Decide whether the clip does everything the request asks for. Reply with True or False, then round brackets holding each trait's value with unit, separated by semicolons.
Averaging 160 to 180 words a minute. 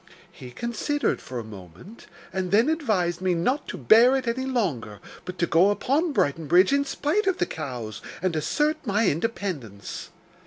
True (170 wpm)